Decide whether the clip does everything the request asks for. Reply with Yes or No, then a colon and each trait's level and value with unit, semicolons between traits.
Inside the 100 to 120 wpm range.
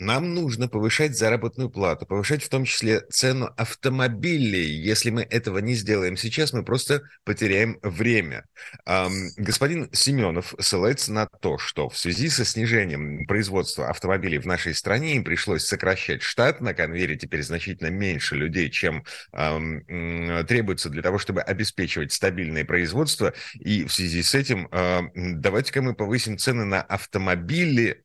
No: average, 145 wpm